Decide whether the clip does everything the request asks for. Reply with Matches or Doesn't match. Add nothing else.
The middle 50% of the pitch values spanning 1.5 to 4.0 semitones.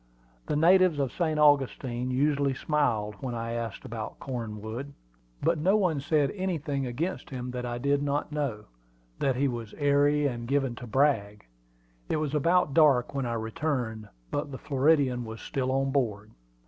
Matches